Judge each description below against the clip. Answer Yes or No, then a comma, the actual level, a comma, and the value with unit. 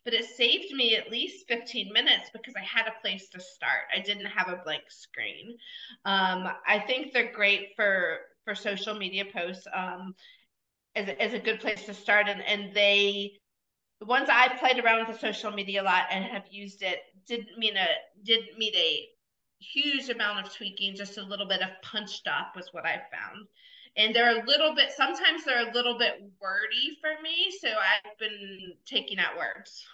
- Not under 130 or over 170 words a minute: No, average, 195 wpm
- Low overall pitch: No, high, 215 Hz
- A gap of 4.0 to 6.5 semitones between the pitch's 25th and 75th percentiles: No, average, 3.4 semitones